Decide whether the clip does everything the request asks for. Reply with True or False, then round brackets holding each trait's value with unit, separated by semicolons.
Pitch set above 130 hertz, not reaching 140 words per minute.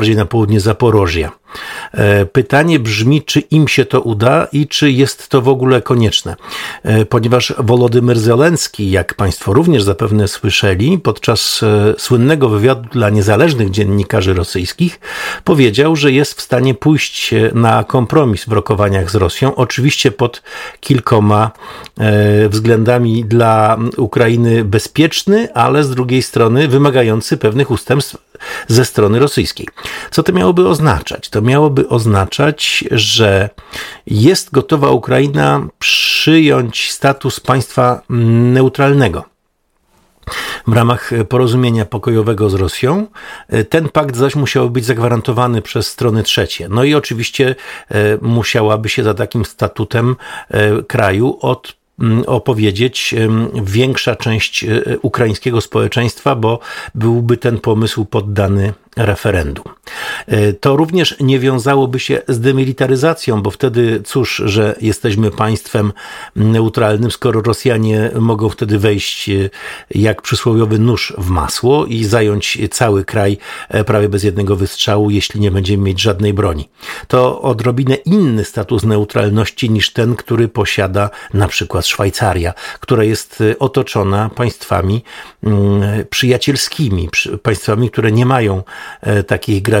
False (115 Hz; 115 wpm)